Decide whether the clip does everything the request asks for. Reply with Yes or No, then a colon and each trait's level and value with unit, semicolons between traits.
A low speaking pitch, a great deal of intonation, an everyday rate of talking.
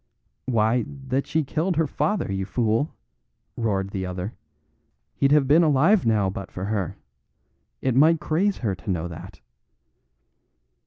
Yes: low, 120 Hz; wide, 7.6 semitones; average, 145 wpm